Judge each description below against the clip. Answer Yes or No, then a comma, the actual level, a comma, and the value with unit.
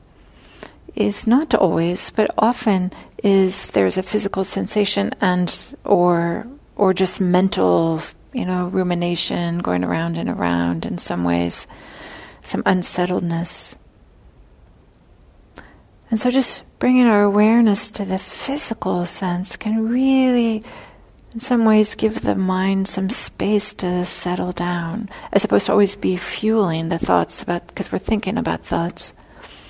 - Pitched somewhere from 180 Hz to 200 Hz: Yes, high, 190 Hz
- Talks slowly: Yes, slow, 130 wpm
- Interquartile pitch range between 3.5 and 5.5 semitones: Yes, average, 4.1 semitones